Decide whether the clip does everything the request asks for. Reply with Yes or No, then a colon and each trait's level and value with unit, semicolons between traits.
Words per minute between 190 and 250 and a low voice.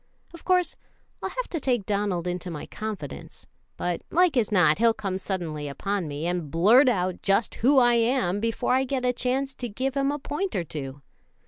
No: average, 200 wpm; high, 215 Hz